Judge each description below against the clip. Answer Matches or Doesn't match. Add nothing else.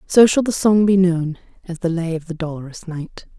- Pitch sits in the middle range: Matches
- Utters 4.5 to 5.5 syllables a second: Matches